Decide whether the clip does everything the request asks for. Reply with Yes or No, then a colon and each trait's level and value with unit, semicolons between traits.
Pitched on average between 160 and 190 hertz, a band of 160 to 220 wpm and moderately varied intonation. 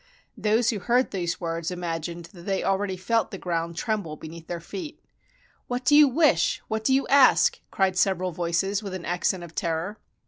Yes: medium, 185 Hz; average, 195 wpm; average, 4.6 semitones